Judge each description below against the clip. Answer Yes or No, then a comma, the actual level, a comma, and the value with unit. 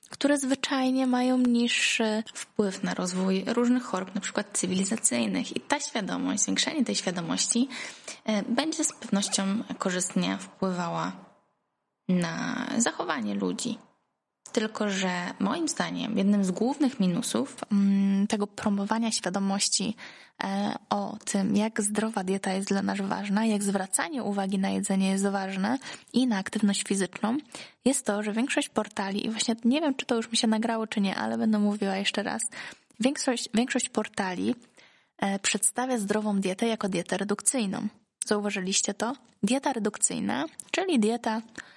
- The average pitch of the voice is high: Yes, high, 215 Hz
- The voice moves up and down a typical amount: Yes, average, 3.5 semitones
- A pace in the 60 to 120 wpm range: No, average, 135 wpm